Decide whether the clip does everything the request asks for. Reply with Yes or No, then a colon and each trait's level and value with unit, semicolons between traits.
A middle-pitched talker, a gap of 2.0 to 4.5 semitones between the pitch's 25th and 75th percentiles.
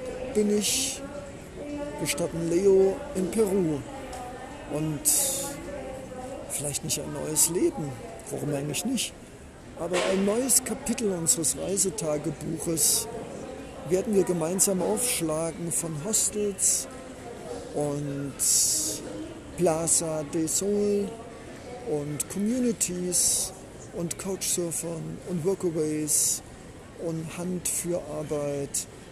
No: medium, 180 Hz; wide, 5.5 semitones